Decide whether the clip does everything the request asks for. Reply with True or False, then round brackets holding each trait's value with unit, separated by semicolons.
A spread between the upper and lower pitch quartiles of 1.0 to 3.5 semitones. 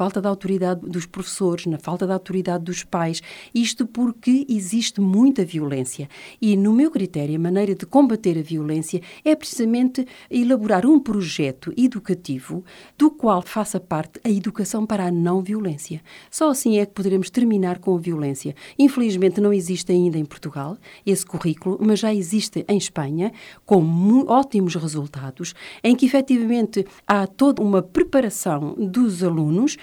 False (4.5 semitones)